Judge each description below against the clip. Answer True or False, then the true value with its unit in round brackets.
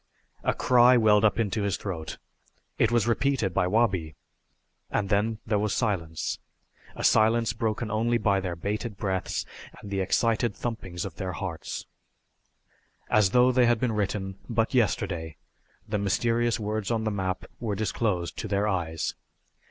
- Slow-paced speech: False (155 wpm)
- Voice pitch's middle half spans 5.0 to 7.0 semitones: False (3.2 semitones)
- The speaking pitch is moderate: False (105 Hz)